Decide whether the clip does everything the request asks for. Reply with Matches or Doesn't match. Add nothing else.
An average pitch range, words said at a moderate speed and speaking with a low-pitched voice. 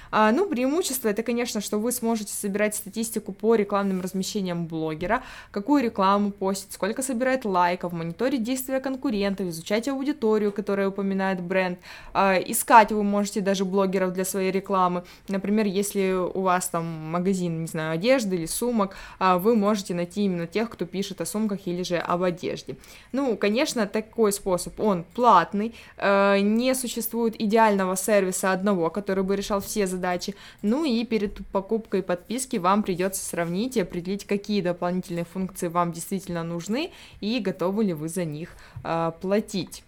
Doesn't match